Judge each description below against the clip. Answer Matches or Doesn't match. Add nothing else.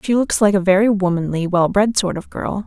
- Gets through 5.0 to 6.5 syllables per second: Matches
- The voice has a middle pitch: Doesn't match